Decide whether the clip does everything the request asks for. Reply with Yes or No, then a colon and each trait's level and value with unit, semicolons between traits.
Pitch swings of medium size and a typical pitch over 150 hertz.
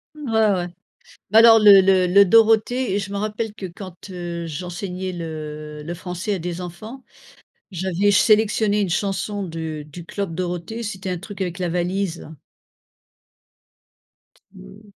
Yes: average, 3.2 semitones; high, 190 Hz